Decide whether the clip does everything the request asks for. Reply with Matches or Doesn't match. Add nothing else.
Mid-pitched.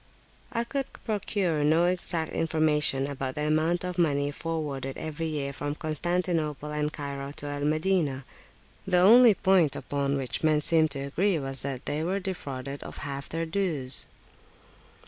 Matches